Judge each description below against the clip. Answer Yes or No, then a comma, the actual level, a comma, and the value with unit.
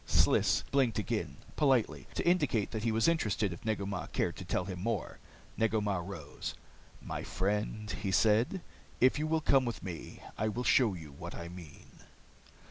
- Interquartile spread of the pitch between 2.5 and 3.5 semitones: No, average, 4.7 semitones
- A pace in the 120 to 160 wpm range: No, average, 180 wpm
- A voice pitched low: Yes, low, 105 Hz